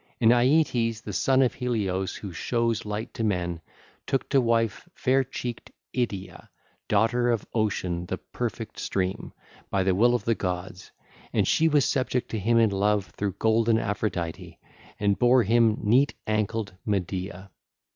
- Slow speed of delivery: No, average, 155 wpm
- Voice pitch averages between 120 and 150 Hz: No, low, 110 Hz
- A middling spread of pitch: Yes, average, 3.9 semitones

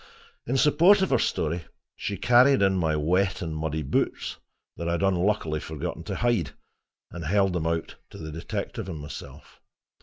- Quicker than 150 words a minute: Yes, average, 175 wpm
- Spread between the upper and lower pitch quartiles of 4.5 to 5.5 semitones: Yes, average, 4.8 semitones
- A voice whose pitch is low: Yes, very low, 85 Hz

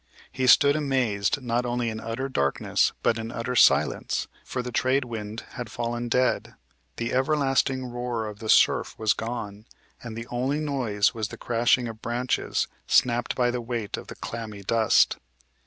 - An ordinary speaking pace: Yes, average, 170 wpm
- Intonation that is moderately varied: No, narrow, 2.2 semitones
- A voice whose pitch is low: Yes, low, 120 Hz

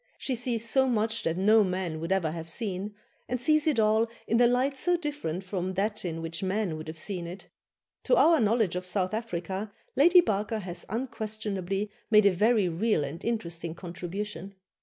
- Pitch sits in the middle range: No, high, 205 Hz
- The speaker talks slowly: No, average, 185 wpm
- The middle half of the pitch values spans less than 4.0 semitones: No, average, 4.4 semitones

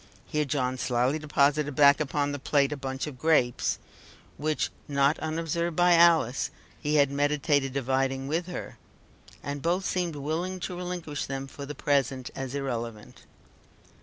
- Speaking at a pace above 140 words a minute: Yes, average, 150 wpm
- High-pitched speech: No, medium, 145 Hz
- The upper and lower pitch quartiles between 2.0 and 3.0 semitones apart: Yes, average, 2.7 semitones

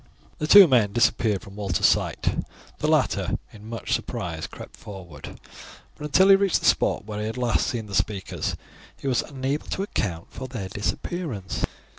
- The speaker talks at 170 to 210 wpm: Yes, average, 175 wpm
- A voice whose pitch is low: Yes, low, 110 Hz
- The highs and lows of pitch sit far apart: Yes, wide, 5.9 semitones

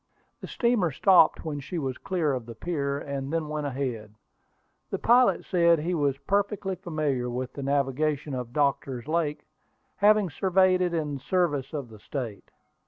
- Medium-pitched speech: Yes, medium, 150 Hz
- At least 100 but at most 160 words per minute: No, average, 170 wpm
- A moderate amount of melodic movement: Yes, average, 4.7 semitones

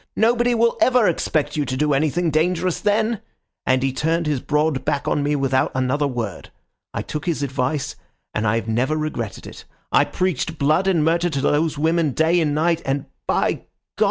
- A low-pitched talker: No, medium, 150 Hz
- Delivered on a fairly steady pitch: No, average, 3.8 semitones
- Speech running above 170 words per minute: Yes, average, 185 wpm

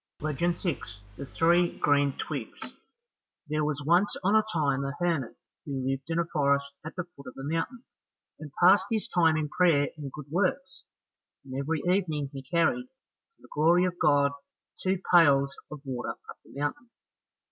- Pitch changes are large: No, average, 4.0 semitones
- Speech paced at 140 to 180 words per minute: Yes, average, 175 wpm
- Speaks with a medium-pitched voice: Yes, medium, 155 Hz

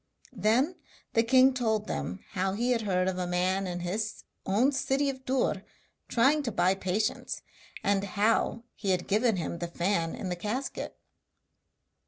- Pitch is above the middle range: Yes, high, 210 Hz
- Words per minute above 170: No, average, 165 wpm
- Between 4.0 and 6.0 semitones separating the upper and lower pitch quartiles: Yes, average, 4.7 semitones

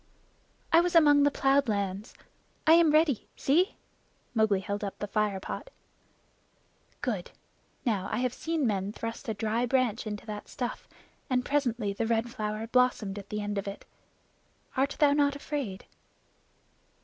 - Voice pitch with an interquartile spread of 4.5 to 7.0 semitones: Yes, wide, 5.4 semitones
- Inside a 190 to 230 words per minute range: No, average, 155 wpm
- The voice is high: Yes, high, 230 Hz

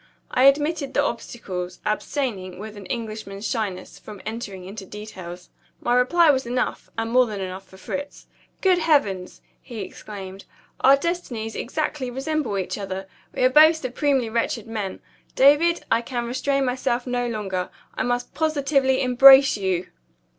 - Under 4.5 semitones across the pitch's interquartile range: No, average, 5.3 semitones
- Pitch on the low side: No, high, 240 Hz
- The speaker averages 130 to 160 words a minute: Yes, average, 150 wpm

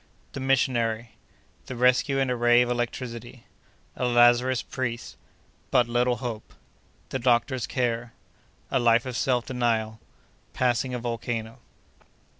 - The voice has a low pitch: Yes, low, 120 Hz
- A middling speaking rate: No, slow, 95 wpm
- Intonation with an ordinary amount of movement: No, narrow, 1.4 semitones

